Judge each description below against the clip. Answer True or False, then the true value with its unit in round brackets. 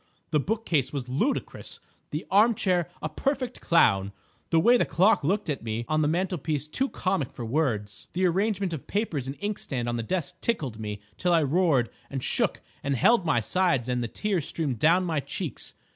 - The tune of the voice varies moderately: False (6.5 semitones)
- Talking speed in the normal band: True (190 wpm)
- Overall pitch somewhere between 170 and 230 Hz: False (160 Hz)